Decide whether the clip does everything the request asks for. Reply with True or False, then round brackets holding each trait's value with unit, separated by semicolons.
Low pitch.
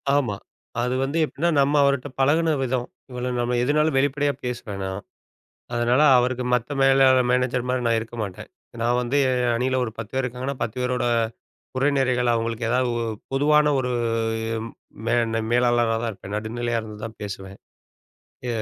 True (125 Hz)